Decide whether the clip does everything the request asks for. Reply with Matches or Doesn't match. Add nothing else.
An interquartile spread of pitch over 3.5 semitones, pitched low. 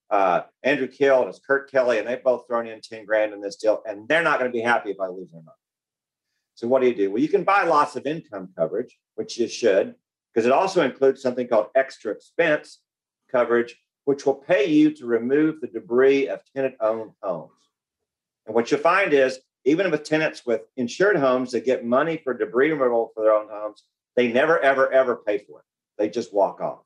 Doesn't match